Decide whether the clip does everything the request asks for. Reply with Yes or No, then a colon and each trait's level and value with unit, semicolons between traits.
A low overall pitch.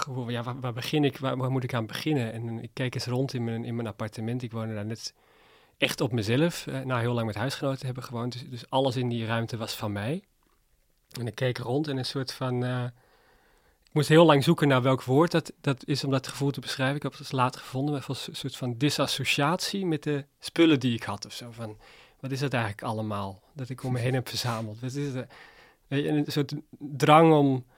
Yes: low, 130 Hz